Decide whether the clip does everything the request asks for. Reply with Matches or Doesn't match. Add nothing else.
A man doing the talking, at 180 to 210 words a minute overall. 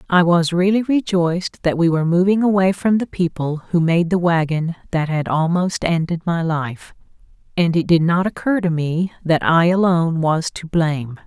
Doesn't match